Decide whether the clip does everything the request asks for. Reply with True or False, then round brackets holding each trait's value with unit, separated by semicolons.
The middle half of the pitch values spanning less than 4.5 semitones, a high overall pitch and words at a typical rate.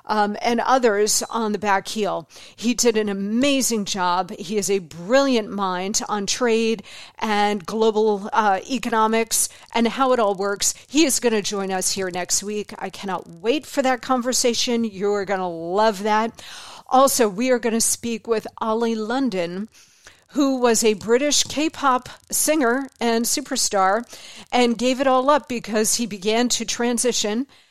True (3.0 semitones; 225 Hz; 165 wpm)